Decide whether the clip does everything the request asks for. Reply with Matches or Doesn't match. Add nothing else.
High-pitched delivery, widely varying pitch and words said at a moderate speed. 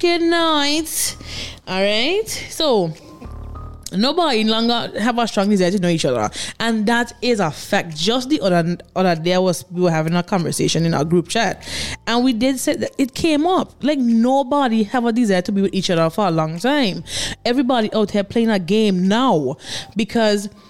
Matches